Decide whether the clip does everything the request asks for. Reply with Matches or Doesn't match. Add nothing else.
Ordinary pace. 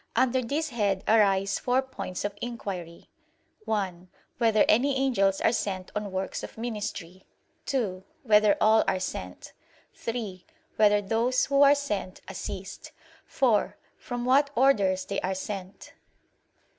Doesn't match